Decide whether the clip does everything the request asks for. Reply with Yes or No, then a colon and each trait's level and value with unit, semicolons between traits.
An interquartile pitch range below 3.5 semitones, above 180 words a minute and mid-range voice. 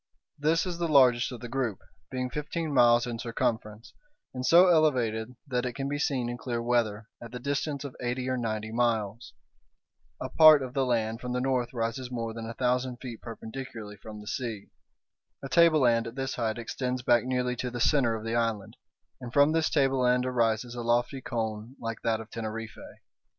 No: narrow, 2.5 semitones; average, 190 wpm; low, 125 Hz